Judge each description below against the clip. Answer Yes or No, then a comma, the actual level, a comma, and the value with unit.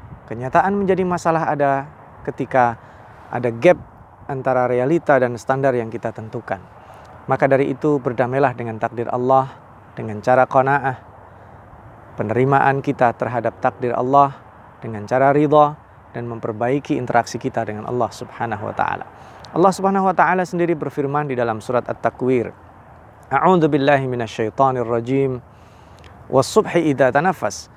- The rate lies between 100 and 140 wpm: Yes, average, 120 wpm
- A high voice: No, low, 125 Hz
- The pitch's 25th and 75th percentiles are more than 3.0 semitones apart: Yes, average, 3.5 semitones